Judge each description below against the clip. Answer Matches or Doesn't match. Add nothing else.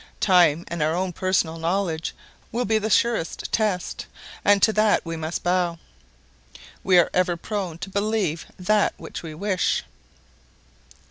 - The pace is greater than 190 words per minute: Doesn't match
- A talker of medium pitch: Matches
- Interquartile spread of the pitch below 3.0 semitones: Doesn't match